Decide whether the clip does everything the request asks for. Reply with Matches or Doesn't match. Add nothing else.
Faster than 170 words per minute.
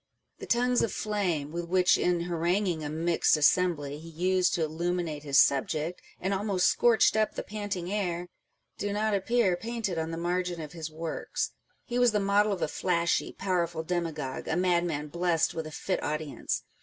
Matches